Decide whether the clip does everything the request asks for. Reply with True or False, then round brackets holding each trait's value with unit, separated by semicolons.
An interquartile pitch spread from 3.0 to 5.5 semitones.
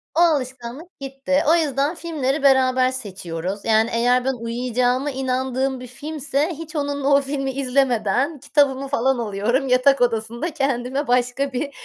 False (2.4 semitones)